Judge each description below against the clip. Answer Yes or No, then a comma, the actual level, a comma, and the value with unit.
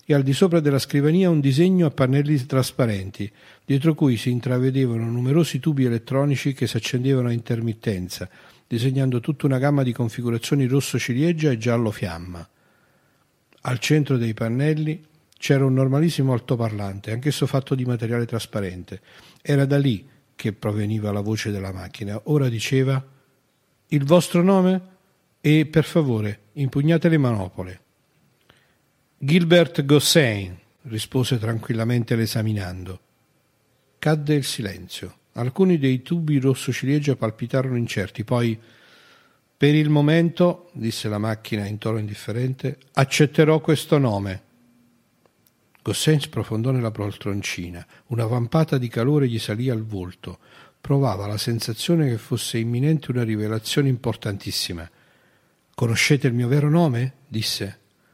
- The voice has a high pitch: No, low, 130 Hz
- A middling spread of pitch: Yes, average, 4.5 semitones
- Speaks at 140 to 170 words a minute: No, average, 125 wpm